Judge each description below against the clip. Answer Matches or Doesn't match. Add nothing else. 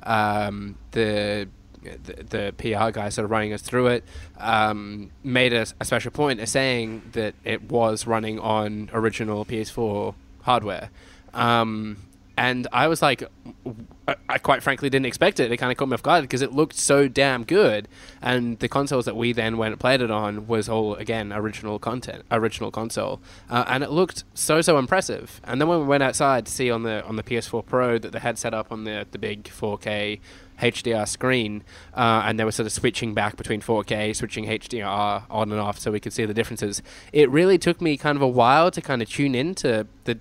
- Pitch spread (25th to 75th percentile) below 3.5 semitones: Matches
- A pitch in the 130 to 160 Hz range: Doesn't match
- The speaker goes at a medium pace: Doesn't match